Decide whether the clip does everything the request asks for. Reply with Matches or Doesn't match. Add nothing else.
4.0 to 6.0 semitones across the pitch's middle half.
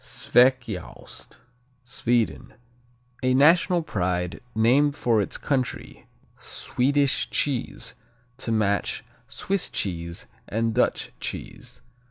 Matches